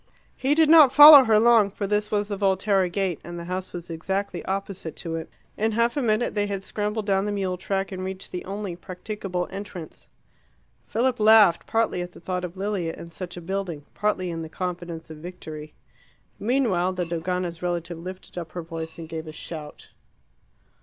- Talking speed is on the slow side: No, average, 195 wpm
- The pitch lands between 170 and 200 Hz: Yes, medium, 185 Hz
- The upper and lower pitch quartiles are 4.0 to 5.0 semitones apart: No, average, 3.3 semitones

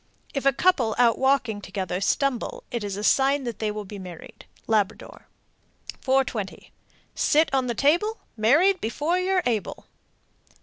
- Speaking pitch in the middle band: No, very high, 250 Hz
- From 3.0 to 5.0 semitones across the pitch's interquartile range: No, wide, 5.4 semitones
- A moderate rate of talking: Yes, average, 145 wpm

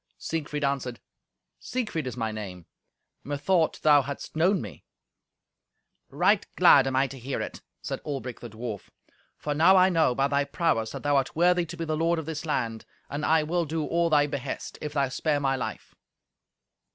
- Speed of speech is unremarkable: Yes, average, 185 wpm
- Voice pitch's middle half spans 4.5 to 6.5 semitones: No, average, 3.6 semitones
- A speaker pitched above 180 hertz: No, medium, 145 Hz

